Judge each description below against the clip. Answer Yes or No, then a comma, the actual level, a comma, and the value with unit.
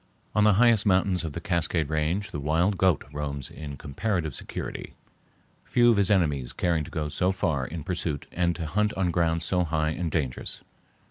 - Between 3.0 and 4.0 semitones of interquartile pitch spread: Yes, average, 3.6 semitones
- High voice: No, very low, 85 Hz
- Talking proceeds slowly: No, average, 190 wpm